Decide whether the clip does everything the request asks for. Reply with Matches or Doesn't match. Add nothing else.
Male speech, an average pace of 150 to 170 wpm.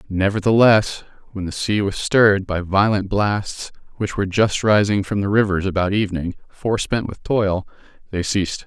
Matches